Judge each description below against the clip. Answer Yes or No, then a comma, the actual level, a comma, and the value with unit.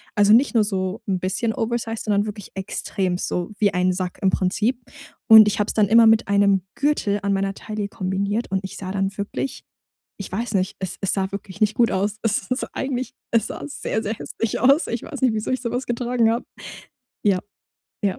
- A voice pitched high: Yes, high, 210 Hz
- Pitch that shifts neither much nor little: Yes, average, 3.0 semitones